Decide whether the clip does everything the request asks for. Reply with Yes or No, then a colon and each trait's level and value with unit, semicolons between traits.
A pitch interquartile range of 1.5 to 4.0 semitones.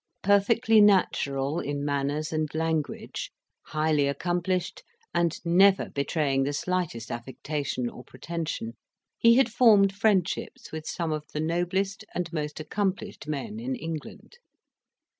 No: average, 5.0 semitones